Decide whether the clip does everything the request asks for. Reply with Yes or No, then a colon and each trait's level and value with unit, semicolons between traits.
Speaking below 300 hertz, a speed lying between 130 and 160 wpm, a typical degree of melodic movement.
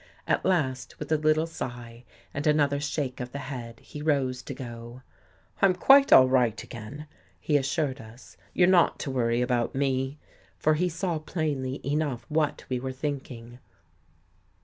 No: low, 135 Hz; average, 170 wpm; average, 3.6 semitones